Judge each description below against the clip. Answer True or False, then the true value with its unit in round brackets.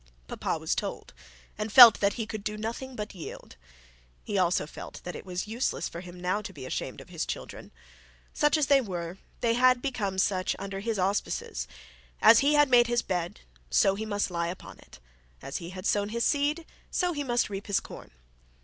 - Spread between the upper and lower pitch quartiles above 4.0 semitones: True (4.6 semitones)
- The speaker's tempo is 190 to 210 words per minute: True (205 wpm)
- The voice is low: False (210 Hz)